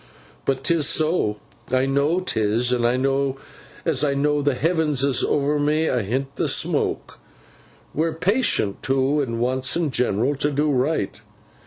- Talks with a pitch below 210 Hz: Yes, medium, 140 Hz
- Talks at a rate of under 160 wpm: Yes, average, 140 wpm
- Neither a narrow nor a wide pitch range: Yes, average, 3.0 semitones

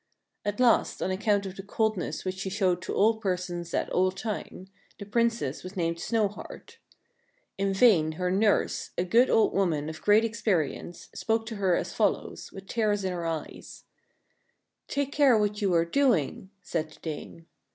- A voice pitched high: Yes, high, 195 Hz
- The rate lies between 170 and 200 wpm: Yes, average, 175 wpm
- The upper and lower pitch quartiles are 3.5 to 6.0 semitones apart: Yes, average, 3.9 semitones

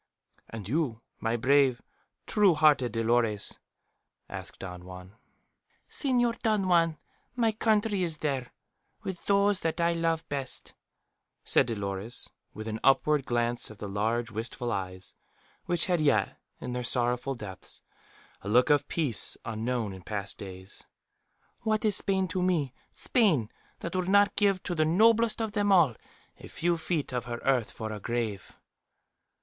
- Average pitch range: No, wide, 8.2 semitones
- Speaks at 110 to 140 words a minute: No, average, 150 wpm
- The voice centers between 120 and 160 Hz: Yes, low, 135 Hz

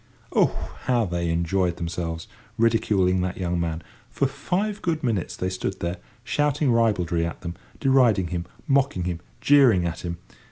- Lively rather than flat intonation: Yes, wide, 7.0 semitones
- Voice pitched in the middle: No, very low, 95 Hz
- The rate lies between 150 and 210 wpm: Yes, average, 155 wpm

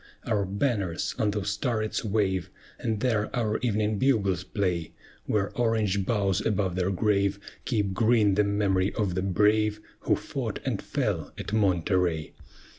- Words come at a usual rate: Yes, average, 145 wpm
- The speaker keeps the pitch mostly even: Yes, narrow, 2.3 semitones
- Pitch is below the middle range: Yes, low, 100 Hz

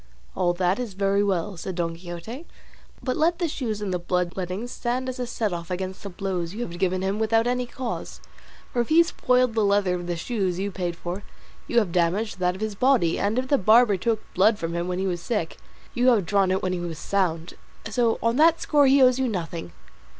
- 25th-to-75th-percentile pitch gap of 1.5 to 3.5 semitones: No, average, 5.1 semitones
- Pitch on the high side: Yes, high, 200 Hz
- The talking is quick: Yes, fast, 230 wpm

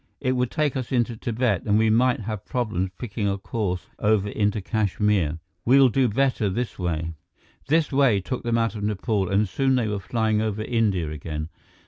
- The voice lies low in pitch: Yes, low, 110 Hz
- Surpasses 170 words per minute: Yes, average, 185 wpm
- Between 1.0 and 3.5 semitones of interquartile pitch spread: No, average, 3.9 semitones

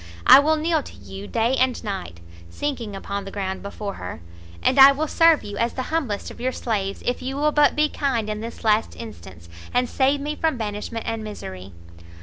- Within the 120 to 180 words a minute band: No, fast, 205 wpm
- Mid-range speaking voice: No, high, 230 Hz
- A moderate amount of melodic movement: No, wide, 5.7 semitones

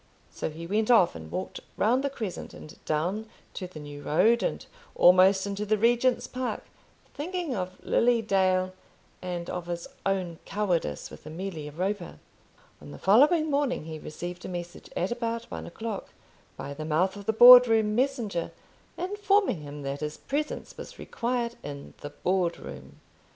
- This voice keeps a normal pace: Yes, average, 165 wpm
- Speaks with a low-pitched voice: No, high, 195 Hz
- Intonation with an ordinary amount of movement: No, wide, 5.8 semitones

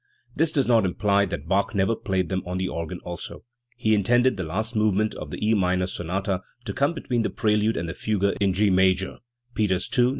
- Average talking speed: No, fast, 220 wpm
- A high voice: No, low, 100 Hz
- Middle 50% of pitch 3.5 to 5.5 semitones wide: No, average, 2.9 semitones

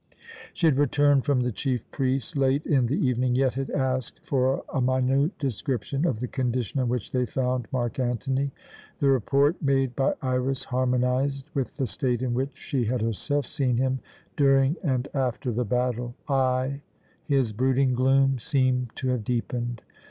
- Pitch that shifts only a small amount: Yes, narrow, 1.6 semitones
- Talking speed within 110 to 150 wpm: No, average, 165 wpm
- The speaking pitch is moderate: No, low, 130 Hz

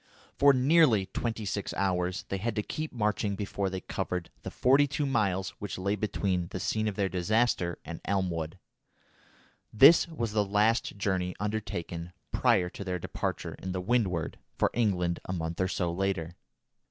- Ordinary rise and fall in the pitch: Yes, average, 3.3 semitones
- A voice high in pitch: No, low, 100 Hz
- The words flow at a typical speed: Yes, average, 165 wpm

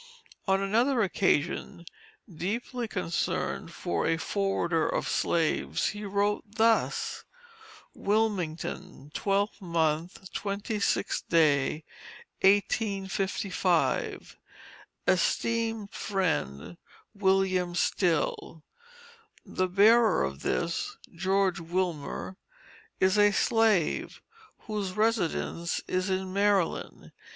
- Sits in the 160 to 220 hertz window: Yes, high, 190 Hz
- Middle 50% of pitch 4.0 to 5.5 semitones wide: No, average, 3.3 semitones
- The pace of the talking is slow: Yes, slow, 80 wpm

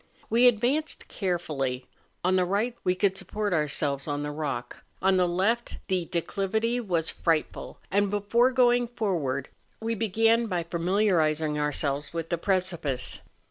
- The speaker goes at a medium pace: Yes, average, 145 wpm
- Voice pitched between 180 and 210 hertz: Yes, medium, 185 Hz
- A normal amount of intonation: No, wide, 6.0 semitones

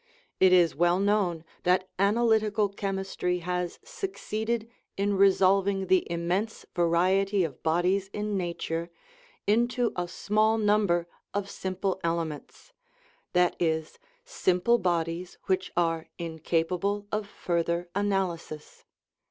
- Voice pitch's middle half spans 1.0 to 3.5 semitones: Yes, average, 3.0 semitones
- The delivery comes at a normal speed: No, slow, 115 wpm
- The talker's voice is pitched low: No, medium, 185 Hz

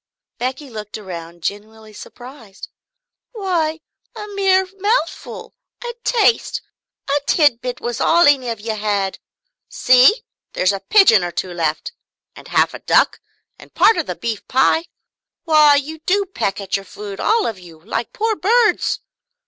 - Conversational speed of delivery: Yes, average, 155 wpm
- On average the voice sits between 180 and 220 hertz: No, very high, 255 Hz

